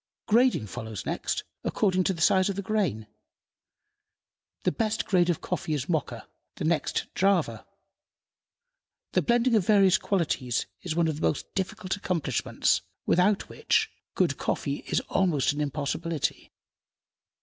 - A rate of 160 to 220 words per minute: No, average, 140 wpm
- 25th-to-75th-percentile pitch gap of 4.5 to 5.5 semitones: Yes, average, 4.8 semitones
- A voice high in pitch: No, medium, 180 Hz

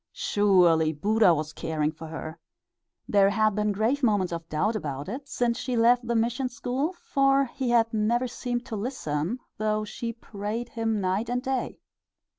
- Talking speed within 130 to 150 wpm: No, average, 170 wpm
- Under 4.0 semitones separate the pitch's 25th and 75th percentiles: No, average, 4.6 semitones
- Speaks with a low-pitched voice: No, high, 220 Hz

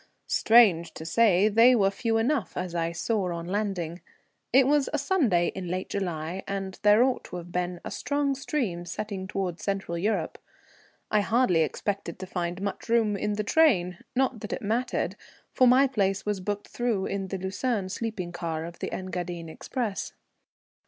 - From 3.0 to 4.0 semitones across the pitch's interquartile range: No, average, 4.5 semitones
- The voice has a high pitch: Yes, high, 195 Hz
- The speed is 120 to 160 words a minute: No, average, 175 wpm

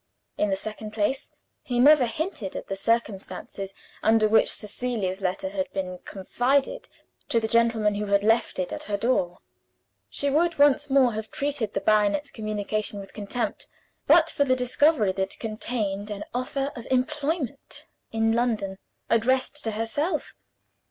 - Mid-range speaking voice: No, high, 225 Hz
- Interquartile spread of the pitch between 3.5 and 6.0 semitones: Yes, average, 4.5 semitones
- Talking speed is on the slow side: No, average, 155 wpm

